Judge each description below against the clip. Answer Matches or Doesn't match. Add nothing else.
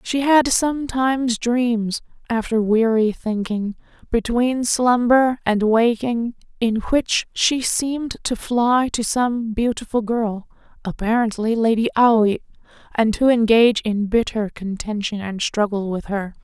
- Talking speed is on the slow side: Matches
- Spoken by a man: Doesn't match